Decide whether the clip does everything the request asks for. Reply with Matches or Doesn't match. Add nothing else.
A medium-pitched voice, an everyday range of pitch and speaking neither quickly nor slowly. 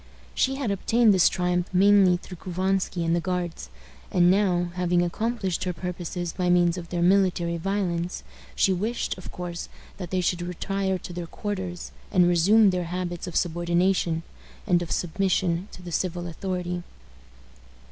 Doesn't match